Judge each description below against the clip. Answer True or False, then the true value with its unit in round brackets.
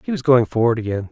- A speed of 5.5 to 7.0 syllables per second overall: True (6.9 syllables/s)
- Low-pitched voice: True (120 Hz)